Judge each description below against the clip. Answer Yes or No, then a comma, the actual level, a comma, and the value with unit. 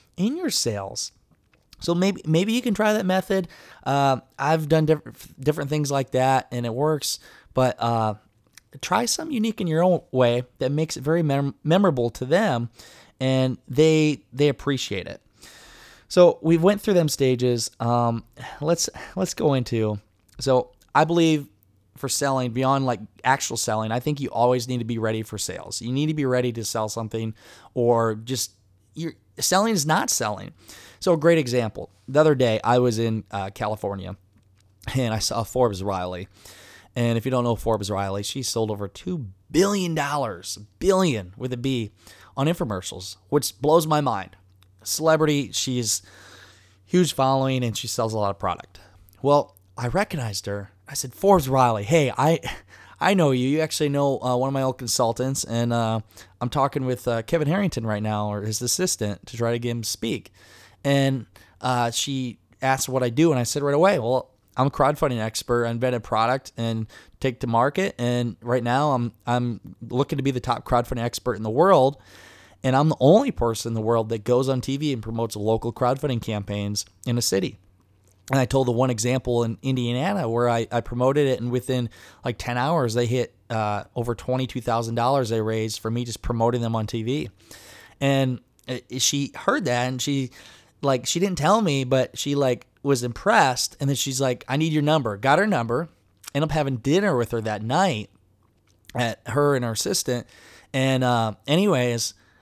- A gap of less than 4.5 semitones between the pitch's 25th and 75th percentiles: Yes, average, 4.1 semitones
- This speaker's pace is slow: No, average, 185 wpm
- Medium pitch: No, low, 125 Hz